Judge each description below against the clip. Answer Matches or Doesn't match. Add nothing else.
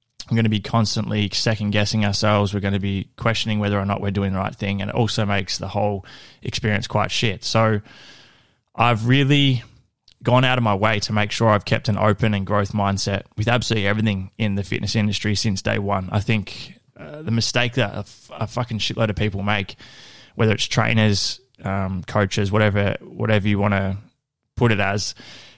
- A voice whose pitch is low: Matches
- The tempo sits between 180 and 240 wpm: Matches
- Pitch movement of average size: Doesn't match